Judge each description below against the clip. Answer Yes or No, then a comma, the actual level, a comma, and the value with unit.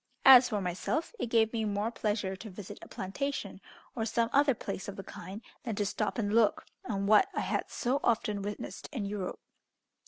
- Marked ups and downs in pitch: No, narrow, 2.6 semitones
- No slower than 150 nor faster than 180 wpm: No, average, 195 wpm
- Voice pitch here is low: No, high, 215 Hz